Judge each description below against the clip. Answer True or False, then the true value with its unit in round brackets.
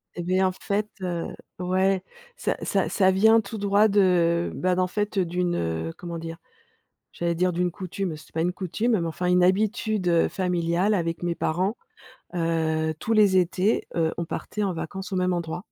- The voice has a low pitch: False (180 Hz)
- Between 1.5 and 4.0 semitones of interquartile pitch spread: True (2.5 semitones)